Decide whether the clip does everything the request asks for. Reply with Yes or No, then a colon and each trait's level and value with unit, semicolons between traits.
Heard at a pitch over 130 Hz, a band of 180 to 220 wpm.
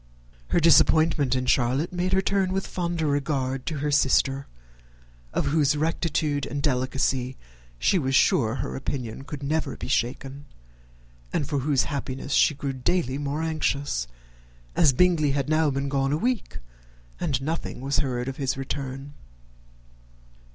No: medium, 140 Hz; average, 150 wpm